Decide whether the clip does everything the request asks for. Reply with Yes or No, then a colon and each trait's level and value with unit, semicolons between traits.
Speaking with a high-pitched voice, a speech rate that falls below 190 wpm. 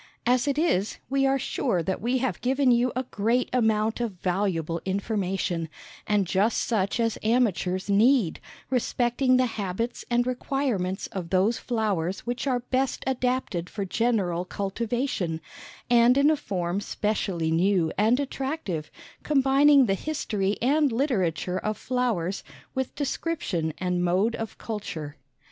Yes: high, 220 Hz; average, 140 wpm